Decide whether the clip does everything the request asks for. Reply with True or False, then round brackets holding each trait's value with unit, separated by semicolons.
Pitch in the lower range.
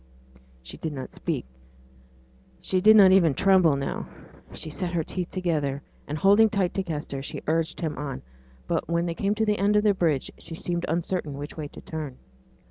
False (170 Hz)